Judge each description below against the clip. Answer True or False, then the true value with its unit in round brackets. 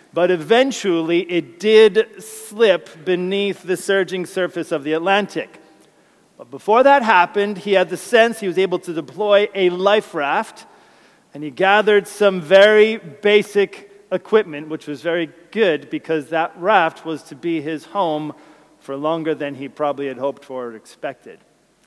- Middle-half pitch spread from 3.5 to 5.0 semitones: True (4.3 semitones)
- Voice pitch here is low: False (180 Hz)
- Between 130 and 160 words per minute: True (155 wpm)